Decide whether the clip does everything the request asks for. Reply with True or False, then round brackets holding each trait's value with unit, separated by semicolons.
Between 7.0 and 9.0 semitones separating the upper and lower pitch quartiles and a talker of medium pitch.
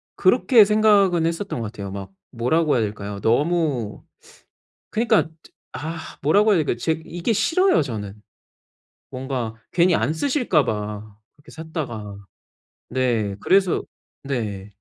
True (8.3 semitones; 145 Hz)